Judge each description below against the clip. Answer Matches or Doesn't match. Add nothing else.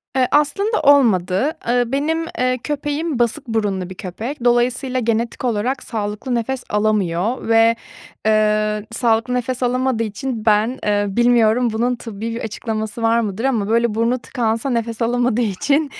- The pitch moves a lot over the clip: Doesn't match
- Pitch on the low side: Doesn't match